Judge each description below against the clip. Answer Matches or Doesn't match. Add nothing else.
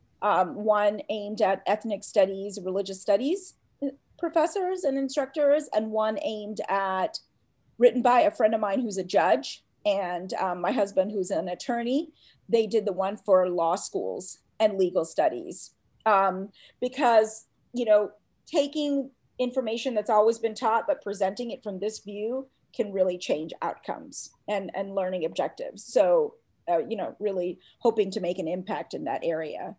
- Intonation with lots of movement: Doesn't match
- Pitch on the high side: Matches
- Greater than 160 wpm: Doesn't match